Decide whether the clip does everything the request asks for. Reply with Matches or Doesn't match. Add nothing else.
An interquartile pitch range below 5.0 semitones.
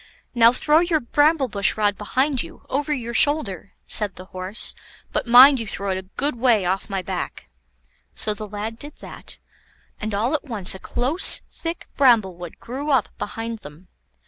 Doesn't match